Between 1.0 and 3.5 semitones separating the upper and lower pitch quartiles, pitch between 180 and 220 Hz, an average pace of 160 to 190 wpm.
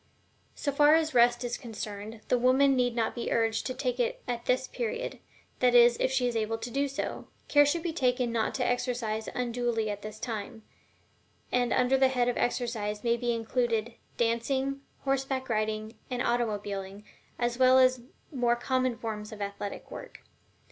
No: narrow, 2.4 semitones; high, 240 Hz; average, 180 wpm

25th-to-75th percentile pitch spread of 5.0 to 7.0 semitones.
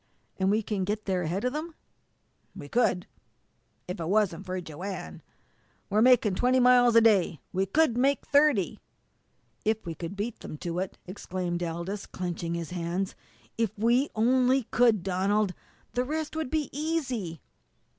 Yes: wide, 5.6 semitones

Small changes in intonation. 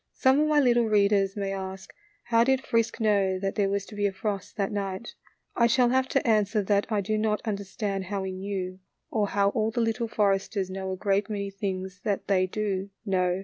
Yes: narrow, 2.2 semitones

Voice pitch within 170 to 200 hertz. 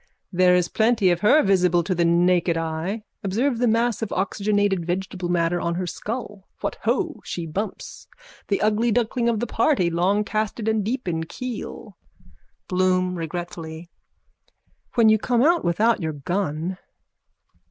Yes: high, 190 Hz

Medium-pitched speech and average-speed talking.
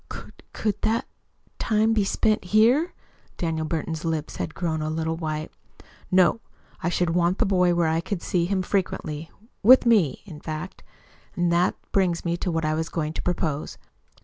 Yes: medium, 175 Hz; average, 175 wpm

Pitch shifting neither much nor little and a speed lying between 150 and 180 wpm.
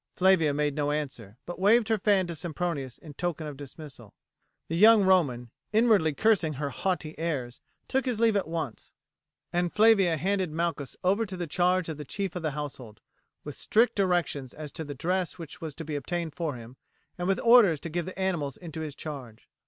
No: average, 4.4 semitones; average, 200 wpm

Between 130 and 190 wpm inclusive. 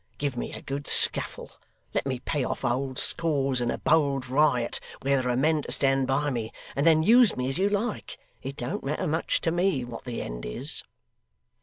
No: fast, 205 wpm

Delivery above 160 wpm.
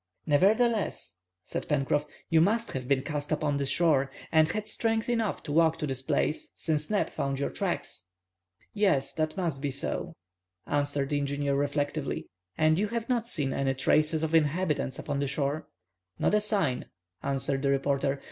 Yes: average, 170 wpm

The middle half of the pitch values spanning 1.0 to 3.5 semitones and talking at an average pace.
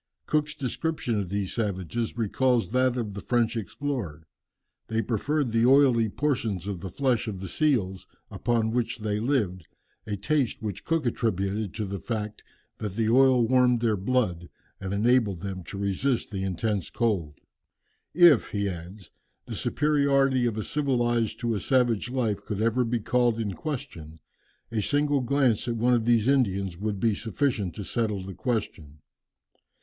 No: average, 4.2 semitones; average, 165 wpm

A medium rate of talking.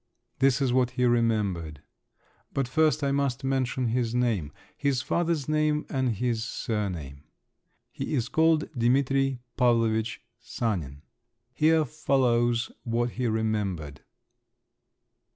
No: slow, 115 wpm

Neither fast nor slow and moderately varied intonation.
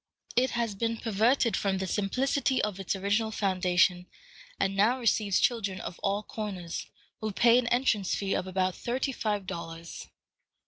Yes: average, 155 wpm; average, 3.6 semitones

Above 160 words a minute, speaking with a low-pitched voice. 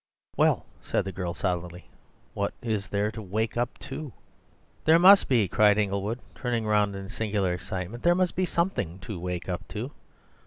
Yes: average, 170 wpm; low, 105 Hz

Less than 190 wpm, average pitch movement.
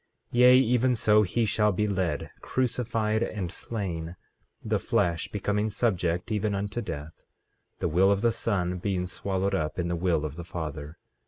Yes: average, 170 wpm; average, 4.1 semitones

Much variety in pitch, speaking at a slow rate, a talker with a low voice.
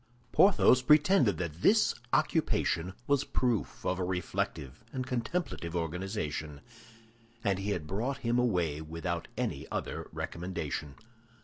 Yes: wide, 7.0 semitones; slow, 120 wpm; very low, 95 Hz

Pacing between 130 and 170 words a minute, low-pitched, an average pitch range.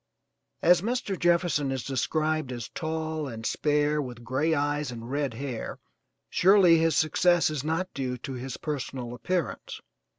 No: average, 145 wpm; medium, 150 Hz; average, 4.0 semitones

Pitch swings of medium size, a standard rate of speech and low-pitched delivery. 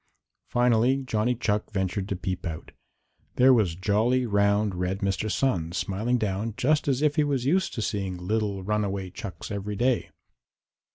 Yes: average, 4.3 semitones; average, 160 wpm; low, 105 Hz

